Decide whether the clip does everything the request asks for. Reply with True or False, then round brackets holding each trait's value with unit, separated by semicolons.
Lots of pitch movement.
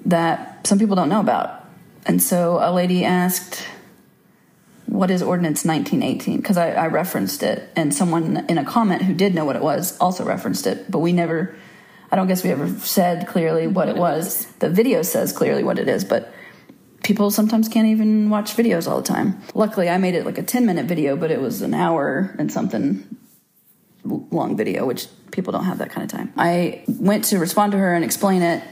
False (3.8 semitones)